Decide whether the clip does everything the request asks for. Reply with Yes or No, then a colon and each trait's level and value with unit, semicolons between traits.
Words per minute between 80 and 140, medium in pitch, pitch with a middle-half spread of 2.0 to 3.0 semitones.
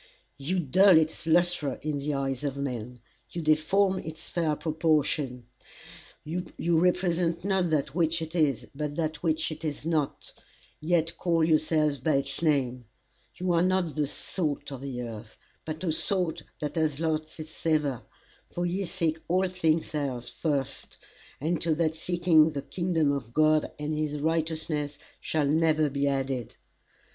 No: average, 155 wpm; medium, 155 Hz; average, 2.7 semitones